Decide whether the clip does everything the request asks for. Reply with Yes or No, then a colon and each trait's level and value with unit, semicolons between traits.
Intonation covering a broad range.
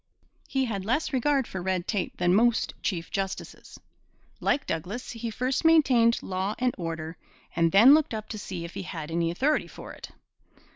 Yes: wide, 6.1 semitones